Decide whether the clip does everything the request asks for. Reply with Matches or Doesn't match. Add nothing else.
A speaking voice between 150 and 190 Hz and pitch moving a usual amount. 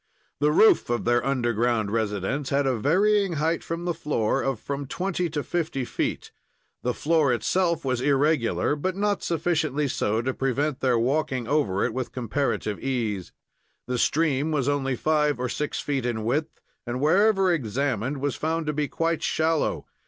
Doesn't match